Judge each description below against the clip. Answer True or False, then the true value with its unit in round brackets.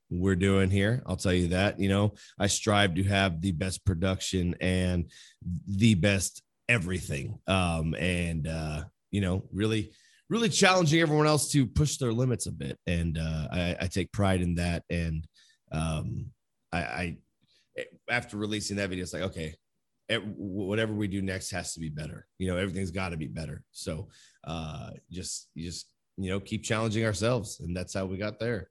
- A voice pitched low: True (95 Hz)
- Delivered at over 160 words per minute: True (180 wpm)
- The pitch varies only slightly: False (3.1 semitones)